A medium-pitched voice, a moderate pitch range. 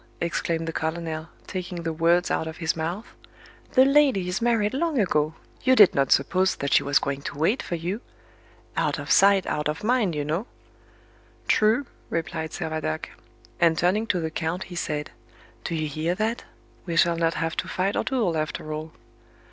Yes: medium, 170 Hz; average, 4.1 semitones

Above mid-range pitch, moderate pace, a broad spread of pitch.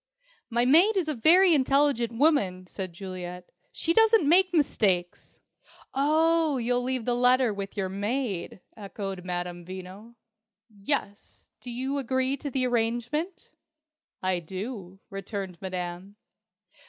No: high, 235 Hz; slow, 125 wpm; wide, 6.8 semitones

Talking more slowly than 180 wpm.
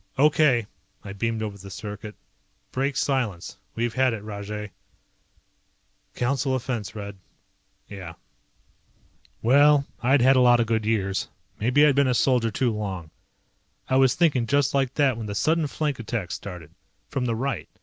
Yes: average, 155 wpm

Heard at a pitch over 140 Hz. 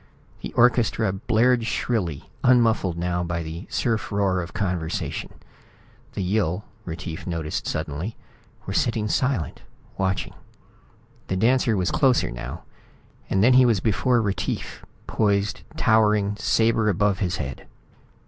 No: low, 100 Hz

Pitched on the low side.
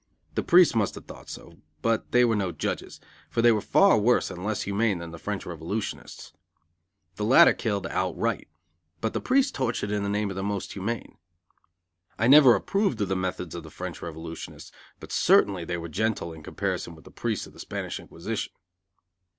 Yes: low, 100 Hz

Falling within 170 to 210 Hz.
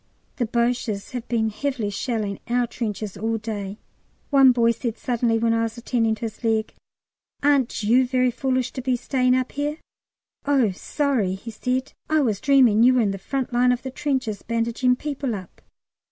No: high, 240 Hz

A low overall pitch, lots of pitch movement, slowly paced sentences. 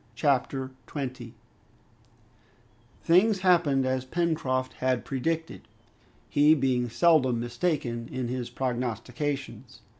No: low, 130 Hz; average, 4.0 semitones; slow, 90 wpm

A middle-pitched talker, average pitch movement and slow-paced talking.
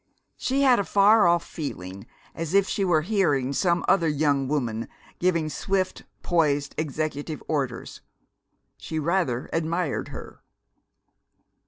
Yes: medium, 160 Hz; average, 4.5 semitones; slow, 125 wpm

